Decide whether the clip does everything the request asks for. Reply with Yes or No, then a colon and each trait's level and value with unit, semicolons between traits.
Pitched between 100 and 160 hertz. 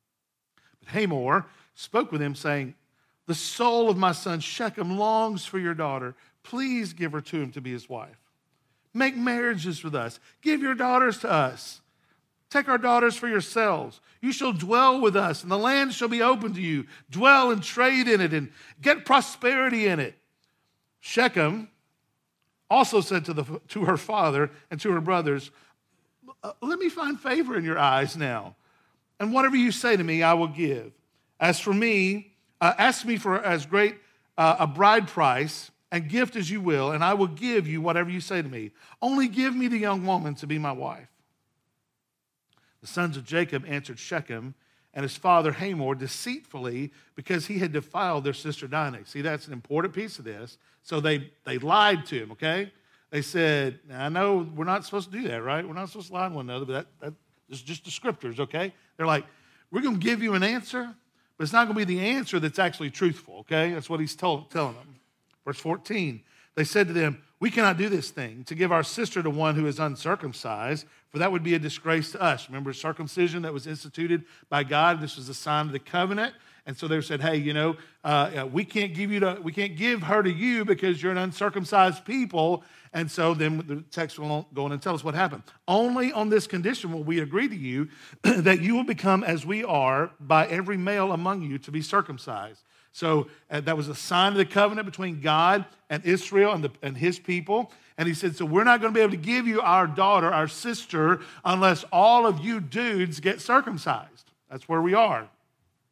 No: medium, 175 Hz